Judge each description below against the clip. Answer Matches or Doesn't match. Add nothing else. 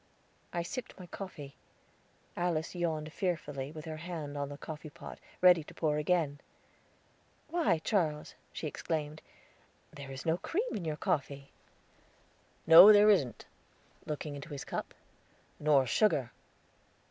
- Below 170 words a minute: Matches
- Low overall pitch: Doesn't match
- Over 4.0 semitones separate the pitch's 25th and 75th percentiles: Doesn't match